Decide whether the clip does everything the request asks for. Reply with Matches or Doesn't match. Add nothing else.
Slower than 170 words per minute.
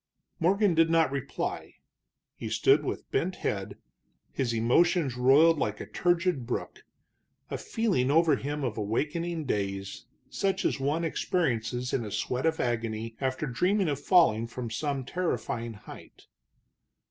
Matches